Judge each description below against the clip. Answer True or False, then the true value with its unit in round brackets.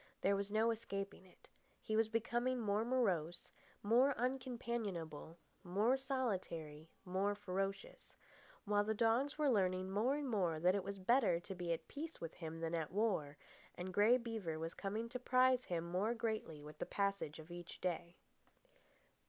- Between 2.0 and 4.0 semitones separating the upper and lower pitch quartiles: False (5.1 semitones)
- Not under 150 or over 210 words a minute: True (165 wpm)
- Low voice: False (200 Hz)